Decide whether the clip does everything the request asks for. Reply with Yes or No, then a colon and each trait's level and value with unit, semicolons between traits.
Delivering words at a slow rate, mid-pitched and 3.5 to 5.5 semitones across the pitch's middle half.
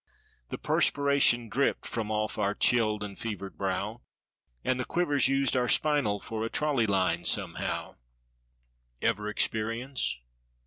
No: slow, 125 wpm; low, 115 Hz; average, 4.4 semitones